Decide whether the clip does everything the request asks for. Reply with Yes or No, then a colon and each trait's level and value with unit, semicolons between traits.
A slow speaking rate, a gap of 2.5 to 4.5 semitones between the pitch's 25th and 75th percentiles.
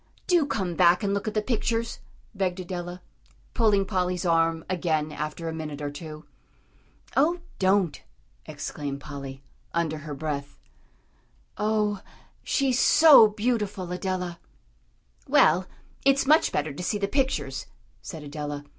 No: slow, 130 wpm; average, 5.3 semitones